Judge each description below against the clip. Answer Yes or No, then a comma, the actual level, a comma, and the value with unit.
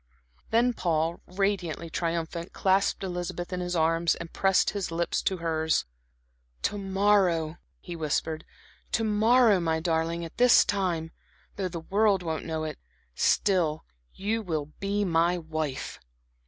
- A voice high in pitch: No, medium, 175 Hz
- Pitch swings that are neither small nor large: Yes, average, 3.4 semitones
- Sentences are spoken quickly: No, average, 140 wpm